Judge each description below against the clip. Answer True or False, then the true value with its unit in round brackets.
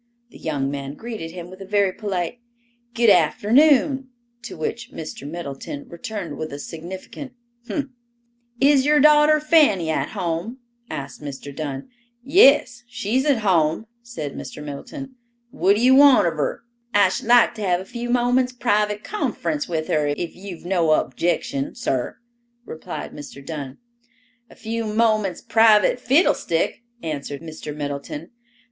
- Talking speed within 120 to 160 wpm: True (145 wpm)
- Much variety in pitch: True (7.7 semitones)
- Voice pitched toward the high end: True (200 Hz)